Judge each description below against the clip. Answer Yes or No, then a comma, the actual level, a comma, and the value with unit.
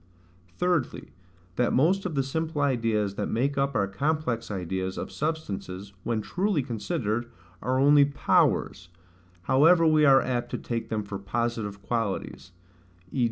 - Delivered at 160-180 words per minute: No, average, 145 wpm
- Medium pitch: No, low, 125 Hz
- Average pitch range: No, wide, 5.8 semitones